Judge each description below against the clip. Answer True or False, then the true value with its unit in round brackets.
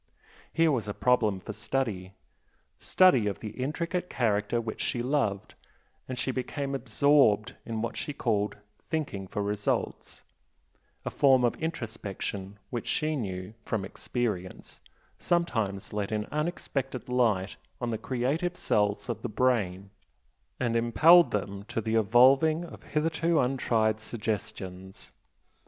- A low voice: True (115 Hz)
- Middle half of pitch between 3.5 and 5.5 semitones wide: True (4.8 semitones)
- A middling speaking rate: False (130 wpm)